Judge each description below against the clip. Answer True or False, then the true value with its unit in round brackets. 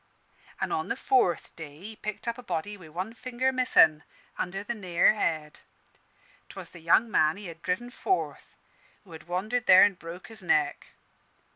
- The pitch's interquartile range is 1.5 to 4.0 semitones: False (5.4 semitones)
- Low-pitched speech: False (185 Hz)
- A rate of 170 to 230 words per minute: True (175 wpm)